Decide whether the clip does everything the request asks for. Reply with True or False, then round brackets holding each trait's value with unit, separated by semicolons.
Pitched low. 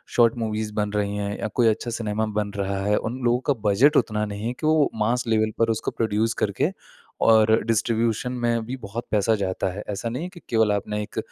True (110 Hz)